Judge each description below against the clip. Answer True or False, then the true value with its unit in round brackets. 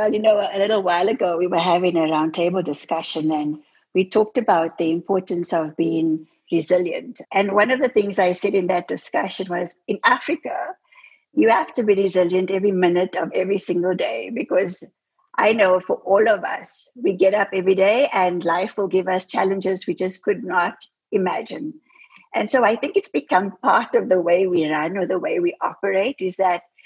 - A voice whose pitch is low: False (185 Hz)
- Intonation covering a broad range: False (3.3 semitones)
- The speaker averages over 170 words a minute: True (195 wpm)